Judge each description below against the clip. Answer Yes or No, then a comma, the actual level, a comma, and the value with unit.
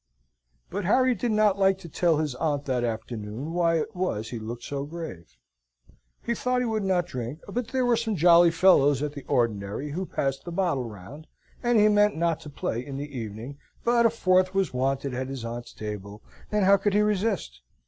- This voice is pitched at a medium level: Yes, medium, 160 Hz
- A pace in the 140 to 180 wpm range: No, fast, 205 wpm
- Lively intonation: Yes, wide, 7.7 semitones